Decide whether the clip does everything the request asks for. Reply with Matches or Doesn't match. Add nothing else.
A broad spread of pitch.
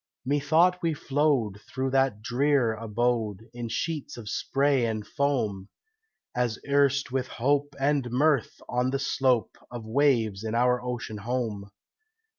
Doesn't match